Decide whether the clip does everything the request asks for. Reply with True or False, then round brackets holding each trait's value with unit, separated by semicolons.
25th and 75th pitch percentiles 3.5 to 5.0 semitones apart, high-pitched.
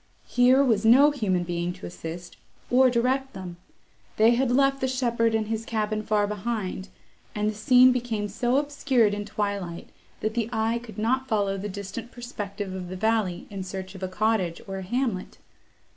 True (3.9 semitones; 215 Hz)